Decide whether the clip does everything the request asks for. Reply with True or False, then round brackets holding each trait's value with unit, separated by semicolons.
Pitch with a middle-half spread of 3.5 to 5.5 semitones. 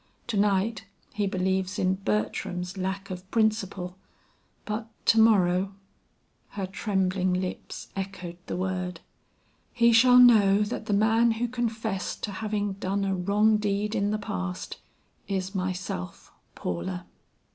False (2.7 semitones)